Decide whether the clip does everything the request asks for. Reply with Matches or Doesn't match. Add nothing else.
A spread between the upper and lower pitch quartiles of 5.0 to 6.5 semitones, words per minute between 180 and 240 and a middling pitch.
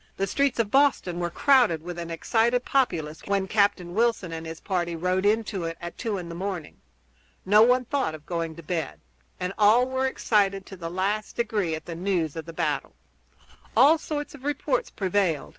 Doesn't match